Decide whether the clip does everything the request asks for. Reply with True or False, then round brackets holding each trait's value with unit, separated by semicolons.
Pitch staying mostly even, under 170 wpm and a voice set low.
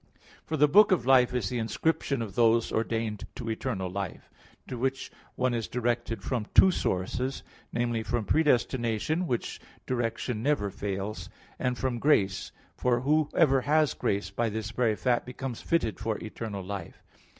False (3.3 semitones; 155 wpm; 120 Hz)